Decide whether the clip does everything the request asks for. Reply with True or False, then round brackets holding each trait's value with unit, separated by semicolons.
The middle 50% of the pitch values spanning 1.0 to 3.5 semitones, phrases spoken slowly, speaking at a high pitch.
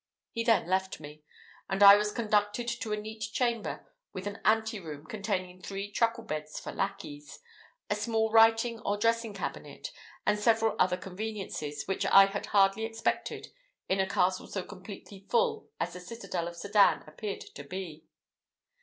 False (3.2 semitones; 160 wpm; 205 Hz)